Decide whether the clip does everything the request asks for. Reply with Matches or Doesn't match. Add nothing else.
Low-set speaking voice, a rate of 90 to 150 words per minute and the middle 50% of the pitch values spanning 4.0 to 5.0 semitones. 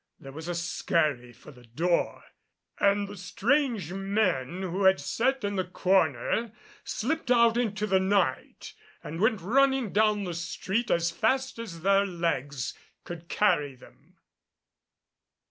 Doesn't match